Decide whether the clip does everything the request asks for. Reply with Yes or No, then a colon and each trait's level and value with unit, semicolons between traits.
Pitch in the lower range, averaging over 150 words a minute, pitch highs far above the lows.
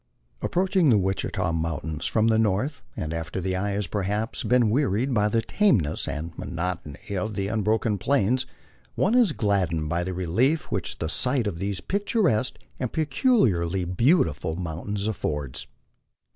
Yes: low, 100 Hz; average, 160 wpm; wide, 6.6 semitones